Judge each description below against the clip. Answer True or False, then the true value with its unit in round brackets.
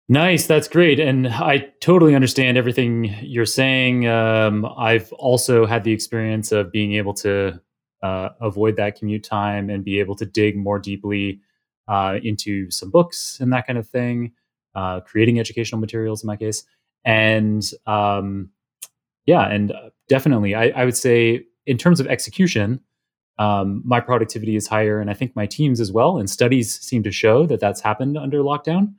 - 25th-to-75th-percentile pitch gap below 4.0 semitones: True (3.5 semitones)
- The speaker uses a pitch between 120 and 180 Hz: False (110 Hz)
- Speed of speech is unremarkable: True (170 wpm)